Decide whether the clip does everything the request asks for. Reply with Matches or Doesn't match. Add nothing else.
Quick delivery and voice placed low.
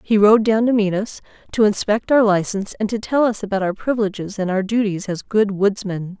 Doesn't match